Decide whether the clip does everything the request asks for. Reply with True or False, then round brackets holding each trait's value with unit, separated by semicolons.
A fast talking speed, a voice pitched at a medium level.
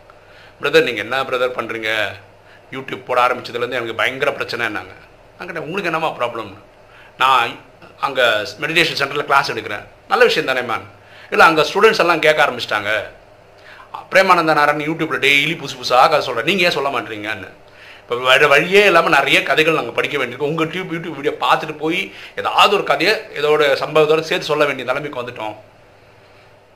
True (155 wpm; 145 Hz)